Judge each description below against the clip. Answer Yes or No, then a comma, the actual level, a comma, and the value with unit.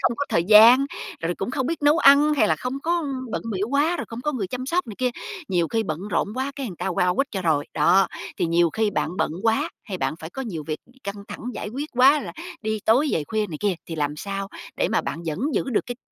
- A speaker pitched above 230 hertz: No, high, 220 Hz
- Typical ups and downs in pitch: No, wide, 7.2 semitones